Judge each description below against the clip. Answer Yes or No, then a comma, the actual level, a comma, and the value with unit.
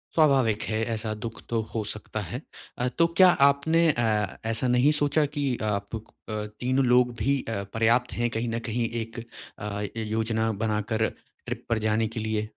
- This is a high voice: No, low, 115 Hz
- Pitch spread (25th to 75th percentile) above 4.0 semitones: No, narrow, 2.4 semitones